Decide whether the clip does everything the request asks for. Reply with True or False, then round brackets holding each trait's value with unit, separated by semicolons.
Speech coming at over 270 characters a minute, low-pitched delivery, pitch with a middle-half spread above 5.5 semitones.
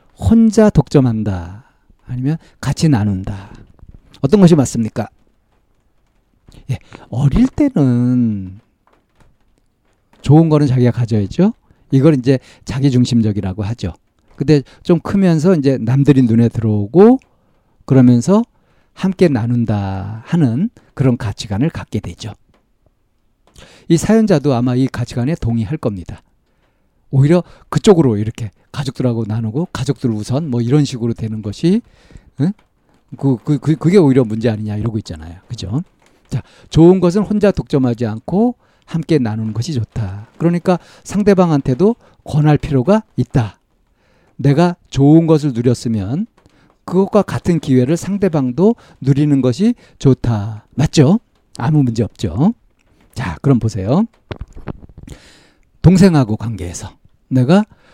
False (265 characters per minute; 130 Hz; 6.5 semitones)